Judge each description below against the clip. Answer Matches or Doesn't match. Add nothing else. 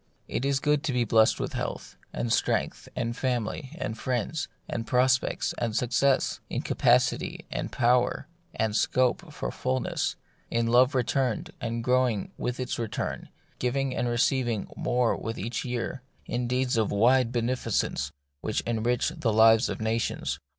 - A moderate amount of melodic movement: Doesn't match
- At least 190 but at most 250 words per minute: Doesn't match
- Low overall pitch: Matches